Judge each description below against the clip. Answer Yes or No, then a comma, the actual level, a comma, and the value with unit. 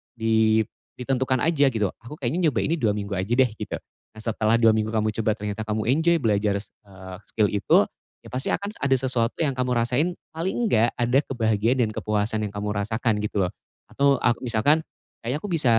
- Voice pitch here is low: Yes, low, 115 Hz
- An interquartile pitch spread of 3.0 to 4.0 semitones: Yes, average, 3.6 semitones